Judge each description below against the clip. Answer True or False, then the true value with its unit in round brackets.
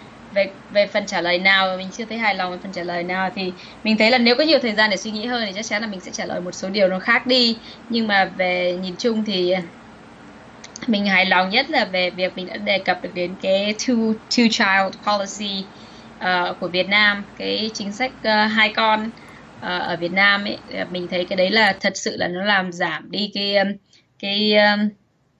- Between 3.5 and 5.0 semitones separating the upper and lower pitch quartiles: False (2.9 semitones)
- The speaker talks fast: False (230 wpm)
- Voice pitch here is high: True (200 Hz)